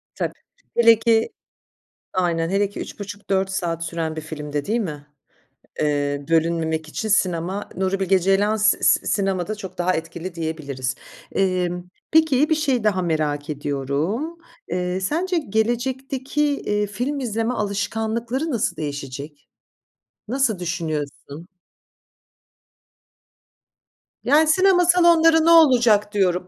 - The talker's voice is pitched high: Yes, high, 195 Hz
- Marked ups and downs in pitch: Yes, wide, 6.6 semitones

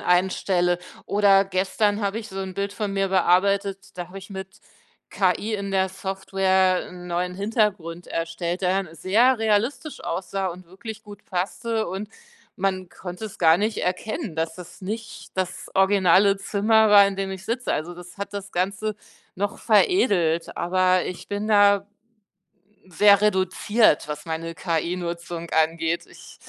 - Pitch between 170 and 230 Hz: Yes, high, 190 Hz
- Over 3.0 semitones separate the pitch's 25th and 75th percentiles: No, narrow, 2.4 semitones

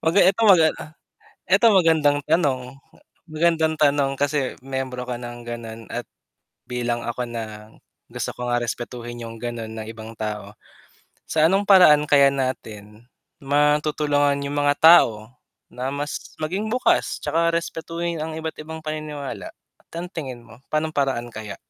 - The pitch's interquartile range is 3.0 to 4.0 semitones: No, average, 4.9 semitones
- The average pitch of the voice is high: No, medium, 140 Hz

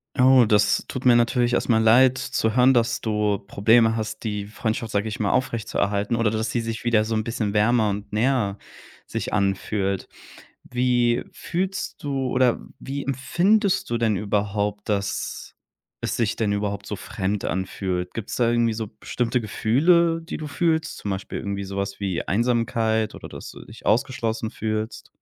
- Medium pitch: No, low, 110 Hz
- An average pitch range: Yes, average, 3.1 semitones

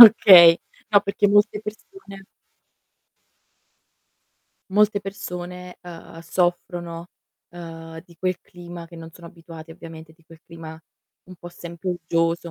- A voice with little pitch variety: Yes, narrow, 2.2 semitones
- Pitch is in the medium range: Yes, medium, 175 Hz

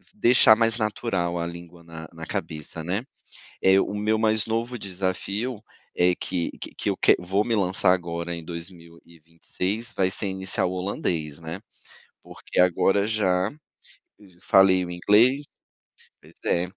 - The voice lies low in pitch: Yes, very low, 95 Hz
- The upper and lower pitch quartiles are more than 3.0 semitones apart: Yes, average, 3.7 semitones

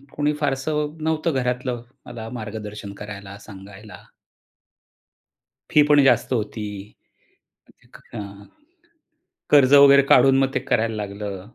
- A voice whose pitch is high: No, low, 120 Hz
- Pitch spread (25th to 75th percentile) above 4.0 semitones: Yes, average, 5.2 semitones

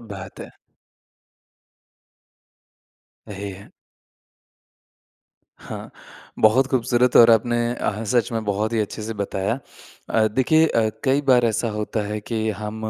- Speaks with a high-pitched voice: No, low, 110 Hz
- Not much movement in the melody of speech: Yes, narrow, 2.3 semitones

